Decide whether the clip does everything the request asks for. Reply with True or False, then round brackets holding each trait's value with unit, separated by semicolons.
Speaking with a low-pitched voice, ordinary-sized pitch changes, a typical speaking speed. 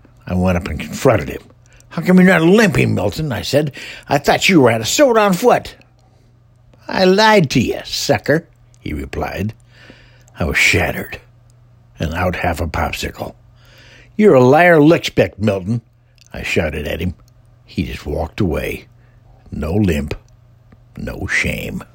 True (120 Hz; 4.1 semitones; 150 wpm)